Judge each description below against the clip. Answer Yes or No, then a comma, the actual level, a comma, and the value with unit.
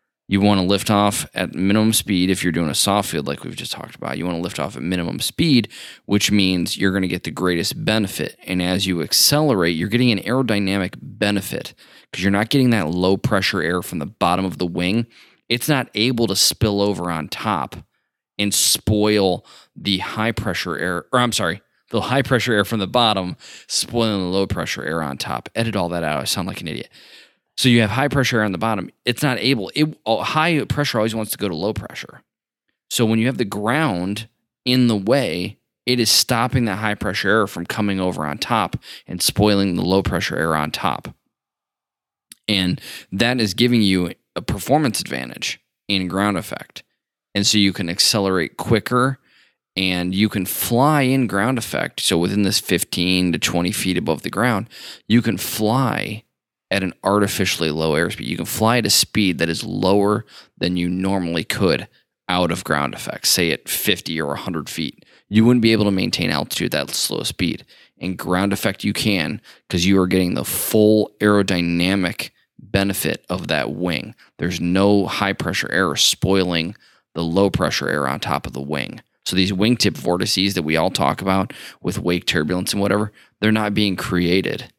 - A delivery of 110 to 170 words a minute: No, average, 195 wpm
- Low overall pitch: Yes, low, 100 Hz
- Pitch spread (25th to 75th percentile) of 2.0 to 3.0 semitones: No, average, 3.7 semitones